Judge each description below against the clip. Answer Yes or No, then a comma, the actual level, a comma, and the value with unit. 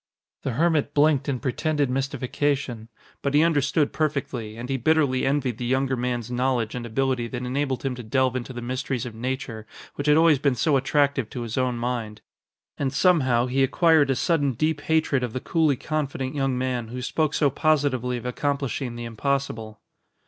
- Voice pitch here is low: Yes, low, 130 Hz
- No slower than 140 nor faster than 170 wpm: No, average, 185 wpm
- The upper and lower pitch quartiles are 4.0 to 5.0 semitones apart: No, average, 2.7 semitones